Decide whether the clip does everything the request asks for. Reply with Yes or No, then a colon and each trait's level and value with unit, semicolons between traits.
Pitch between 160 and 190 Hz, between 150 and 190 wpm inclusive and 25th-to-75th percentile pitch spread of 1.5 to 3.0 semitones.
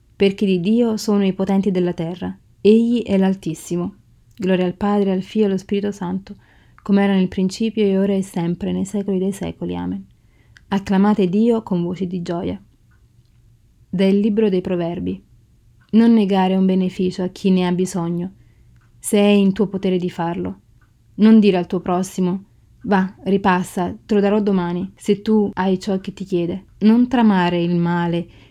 Yes: medium, 185 Hz; fast, 170 wpm; narrow, 2.6 semitones